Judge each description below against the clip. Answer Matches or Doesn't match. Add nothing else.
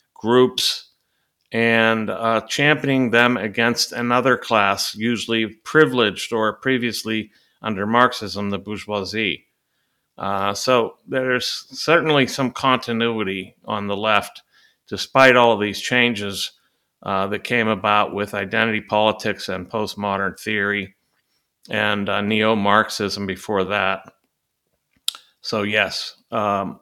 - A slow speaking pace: Matches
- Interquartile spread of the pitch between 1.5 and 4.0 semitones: Matches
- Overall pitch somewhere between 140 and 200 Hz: Doesn't match